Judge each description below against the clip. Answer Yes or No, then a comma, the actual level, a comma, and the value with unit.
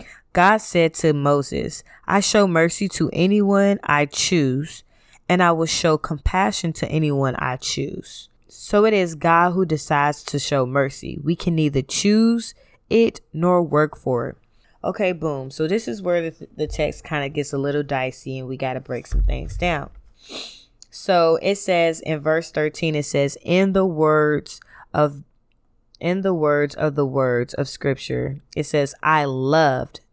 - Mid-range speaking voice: Yes, medium, 155 Hz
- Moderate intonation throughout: Yes, average, 3.6 semitones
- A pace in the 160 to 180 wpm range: Yes, average, 170 wpm